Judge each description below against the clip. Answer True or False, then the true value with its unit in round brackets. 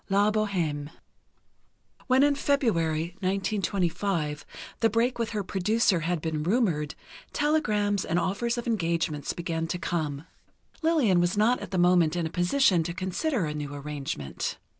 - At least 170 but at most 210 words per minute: False (150 wpm)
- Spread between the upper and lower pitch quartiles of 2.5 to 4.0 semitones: False (5.2 semitones)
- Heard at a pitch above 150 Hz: True (185 Hz)